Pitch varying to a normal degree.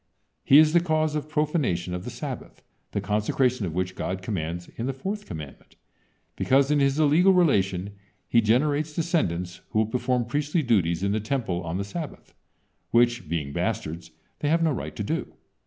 No: wide, 8.7 semitones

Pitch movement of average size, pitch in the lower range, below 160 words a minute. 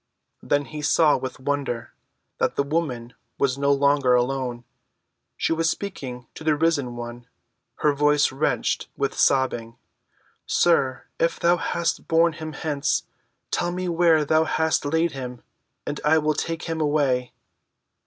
No: average, 3.7 semitones; medium, 145 Hz; average, 145 wpm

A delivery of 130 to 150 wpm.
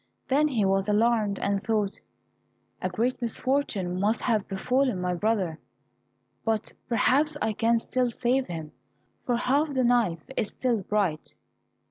Yes: average, 140 wpm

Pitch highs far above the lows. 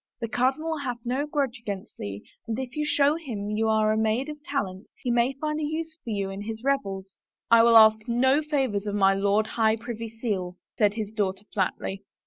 No: average, 4.7 semitones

